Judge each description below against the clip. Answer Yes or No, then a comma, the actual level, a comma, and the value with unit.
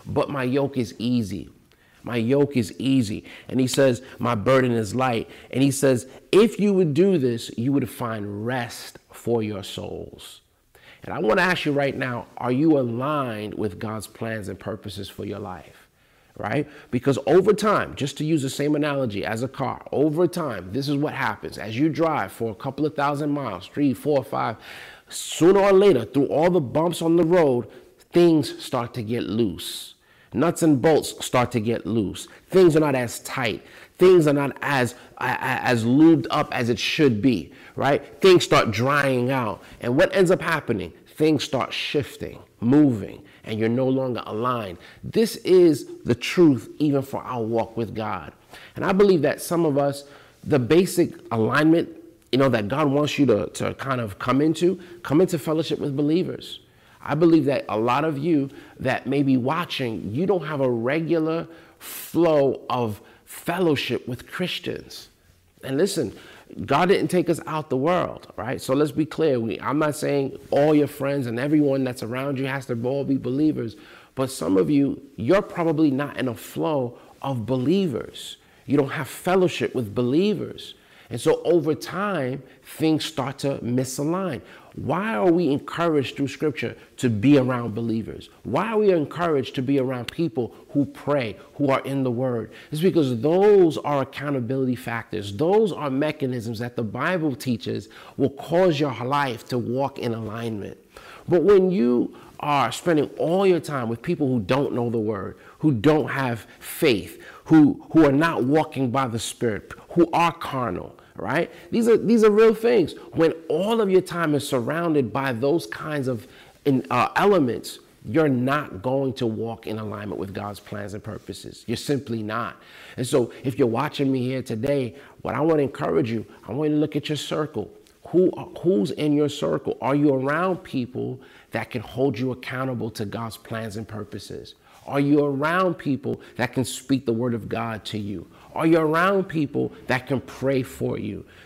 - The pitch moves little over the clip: No, average, 4.7 semitones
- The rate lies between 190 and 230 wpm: No, average, 180 wpm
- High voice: No, low, 135 Hz